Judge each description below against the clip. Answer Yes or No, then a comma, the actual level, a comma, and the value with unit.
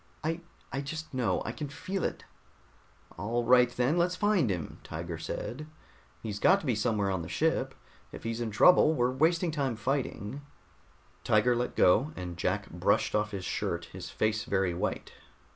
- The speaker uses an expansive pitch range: Yes, wide, 6.5 semitones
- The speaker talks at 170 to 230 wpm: Yes, average, 175 wpm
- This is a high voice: No, low, 120 Hz